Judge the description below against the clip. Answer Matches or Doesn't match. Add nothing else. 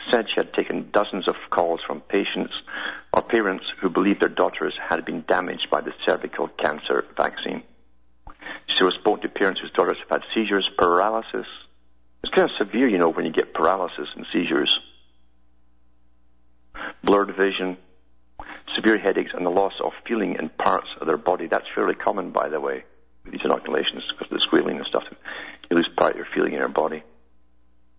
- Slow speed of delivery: Doesn't match